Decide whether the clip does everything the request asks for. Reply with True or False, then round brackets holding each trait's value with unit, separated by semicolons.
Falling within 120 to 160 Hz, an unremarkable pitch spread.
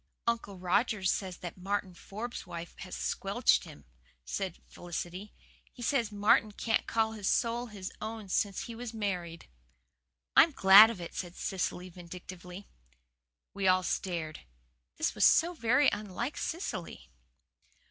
False (195 Hz; 3.8 semitones)